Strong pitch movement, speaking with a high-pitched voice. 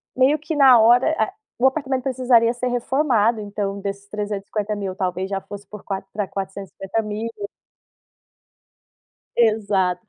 No: average, 3.8 semitones; high, 210 Hz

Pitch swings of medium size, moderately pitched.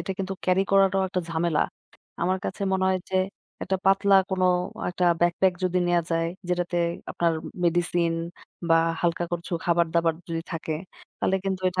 No: narrow, 1.8 semitones; medium, 175 Hz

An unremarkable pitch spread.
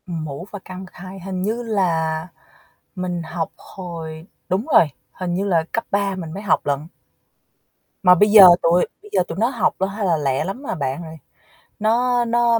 Yes: average, 4.0 semitones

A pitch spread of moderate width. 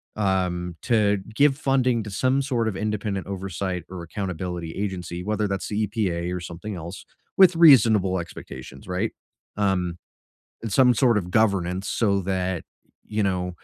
Yes: average, 3.2 semitones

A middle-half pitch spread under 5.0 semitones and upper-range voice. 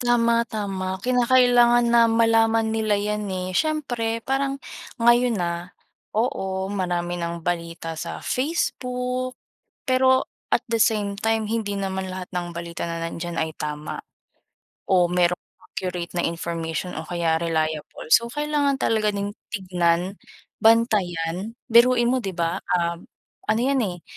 No: average, 5.3 semitones; high, 200 Hz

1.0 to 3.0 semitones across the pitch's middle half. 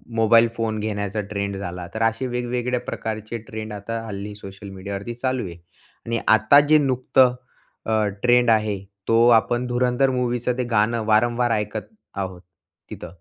Yes: narrow, 2.6 semitones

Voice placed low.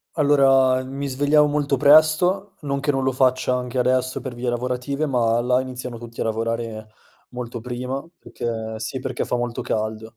Yes: low, 125 Hz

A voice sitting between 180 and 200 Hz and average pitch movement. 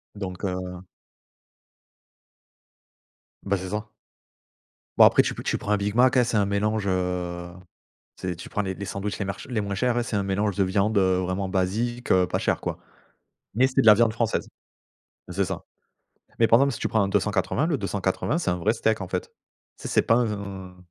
No: low, 100 Hz; average, 3.1 semitones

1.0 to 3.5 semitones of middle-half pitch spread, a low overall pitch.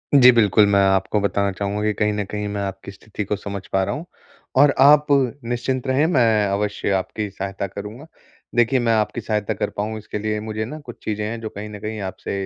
Yes: average, 2.8 semitones; low, 105 Hz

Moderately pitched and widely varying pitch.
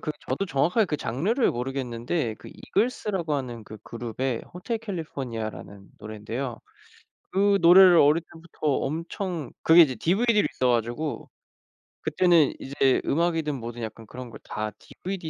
Yes: medium, 145 Hz; wide, 6.5 semitones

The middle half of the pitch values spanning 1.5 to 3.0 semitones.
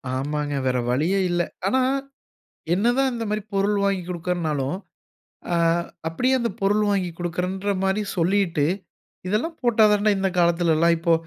No: average, 3.8 semitones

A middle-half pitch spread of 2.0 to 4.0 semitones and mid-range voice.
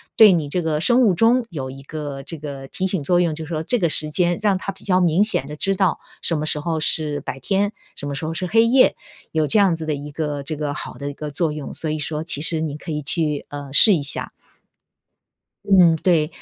Yes: average, 3.7 semitones; medium, 160 Hz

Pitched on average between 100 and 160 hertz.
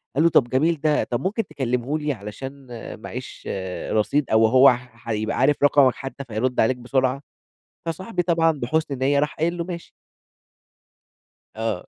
Yes: medium, 140 Hz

